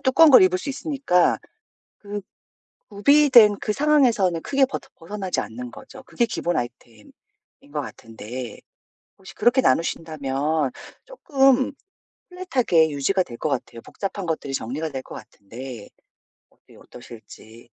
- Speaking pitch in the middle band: Yes, medium, 175 Hz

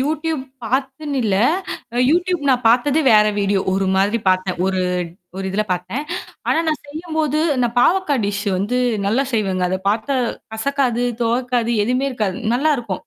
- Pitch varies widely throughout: Yes, wide, 6.0 semitones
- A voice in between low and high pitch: No, high, 240 Hz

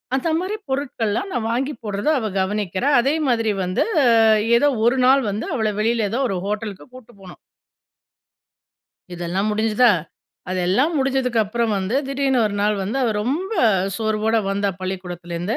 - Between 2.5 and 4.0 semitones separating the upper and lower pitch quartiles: No, average, 4.7 semitones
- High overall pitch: Yes, high, 220 Hz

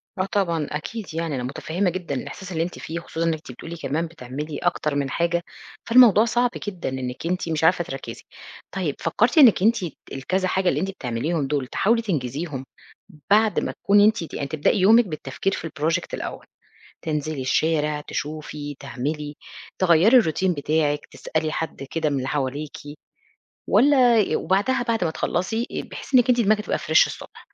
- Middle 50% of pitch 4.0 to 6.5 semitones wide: Yes, average, 5.1 semitones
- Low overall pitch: No, medium, 165 Hz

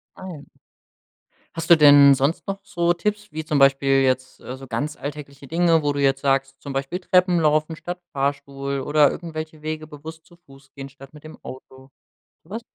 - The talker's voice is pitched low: No, medium, 150 Hz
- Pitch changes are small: No, average, 3.1 semitones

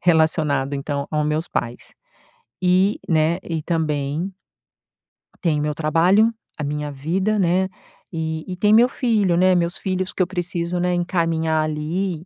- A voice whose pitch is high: No, medium, 170 Hz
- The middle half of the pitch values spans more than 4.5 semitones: No, average, 3.2 semitones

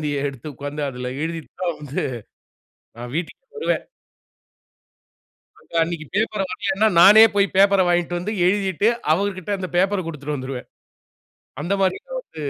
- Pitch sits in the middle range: Yes, medium, 175 Hz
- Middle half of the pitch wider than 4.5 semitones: Yes, average, 5.0 semitones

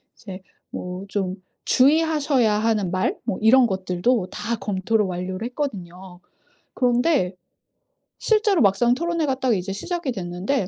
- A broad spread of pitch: Yes, wide, 5.9 semitones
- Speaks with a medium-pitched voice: No, high, 215 Hz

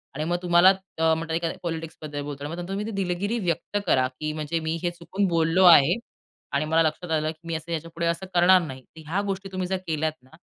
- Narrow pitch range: Yes, narrow, 2.2 semitones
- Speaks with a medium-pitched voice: Yes, medium, 165 Hz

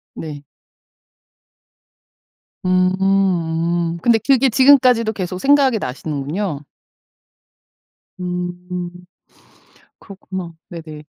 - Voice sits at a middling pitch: Yes, medium, 180 Hz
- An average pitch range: Yes, average, 4.0 semitones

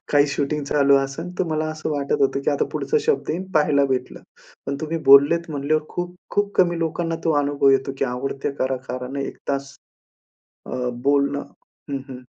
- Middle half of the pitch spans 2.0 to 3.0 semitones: Yes, average, 2.7 semitones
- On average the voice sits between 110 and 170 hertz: Yes, medium, 140 Hz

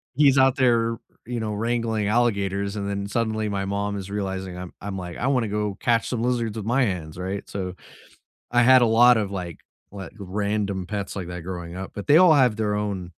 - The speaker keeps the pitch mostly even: No, average, 3.2 semitones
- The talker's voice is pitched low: Yes, low, 105 Hz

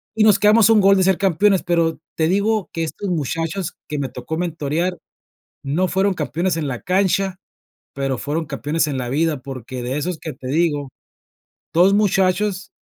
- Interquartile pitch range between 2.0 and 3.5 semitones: No, average, 4.6 semitones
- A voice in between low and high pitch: Yes, medium, 170 Hz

